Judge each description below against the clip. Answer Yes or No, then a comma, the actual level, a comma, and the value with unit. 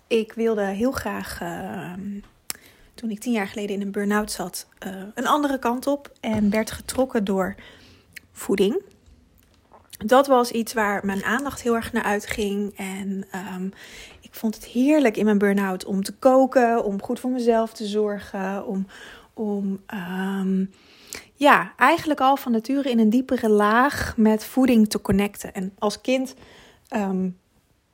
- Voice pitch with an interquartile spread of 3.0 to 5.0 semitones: Yes, average, 3.6 semitones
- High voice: Yes, high, 215 Hz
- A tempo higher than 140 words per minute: Yes, average, 155 wpm